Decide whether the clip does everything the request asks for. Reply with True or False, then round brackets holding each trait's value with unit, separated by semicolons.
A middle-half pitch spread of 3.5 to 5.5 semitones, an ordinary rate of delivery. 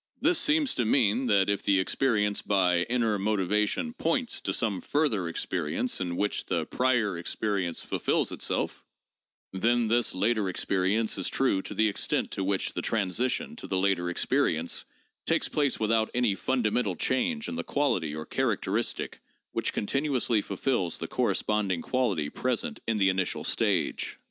True (4.9 semitones; 155 wpm)